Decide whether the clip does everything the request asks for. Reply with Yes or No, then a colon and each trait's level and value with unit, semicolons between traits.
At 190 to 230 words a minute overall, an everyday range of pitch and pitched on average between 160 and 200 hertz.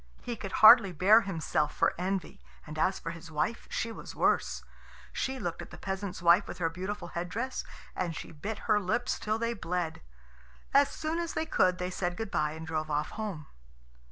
Yes: average, 200 wpm; average, 4.9 semitones; medium, 185 Hz